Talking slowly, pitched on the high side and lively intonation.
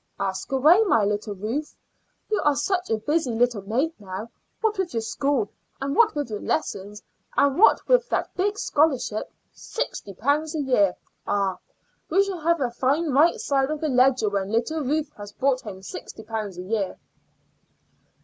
No: average, 175 wpm; very high, 265 Hz; wide, 6.9 semitones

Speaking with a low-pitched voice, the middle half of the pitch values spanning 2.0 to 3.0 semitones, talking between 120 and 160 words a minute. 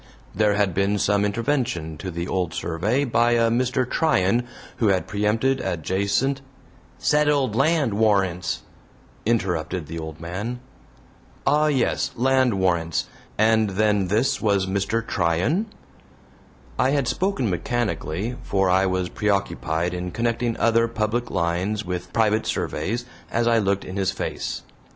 No: low, 105 Hz; average, 4.5 semitones; slow, 135 wpm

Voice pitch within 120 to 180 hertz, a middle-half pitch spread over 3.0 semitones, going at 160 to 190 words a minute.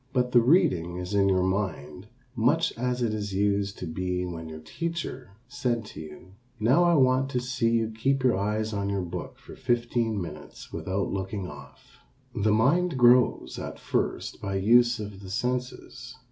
No: low, 110 Hz; average, 4.7 semitones; average, 175 wpm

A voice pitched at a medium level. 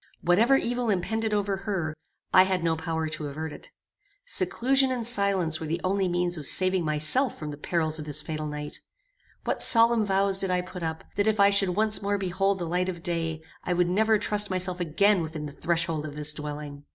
Yes: medium, 180 Hz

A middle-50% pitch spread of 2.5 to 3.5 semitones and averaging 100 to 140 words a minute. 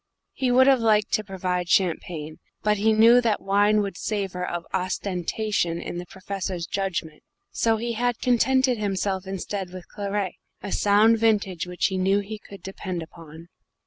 No: average, 3.1 semitones; average, 165 wpm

